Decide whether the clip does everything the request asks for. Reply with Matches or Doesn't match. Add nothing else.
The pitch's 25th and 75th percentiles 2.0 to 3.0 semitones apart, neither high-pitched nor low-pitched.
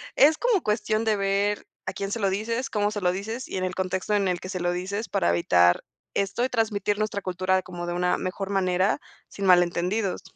Doesn't match